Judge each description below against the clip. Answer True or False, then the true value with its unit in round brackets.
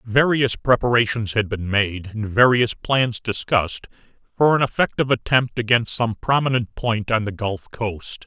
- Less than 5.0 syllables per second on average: True (4.6 syllables/s)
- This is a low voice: True (115 Hz)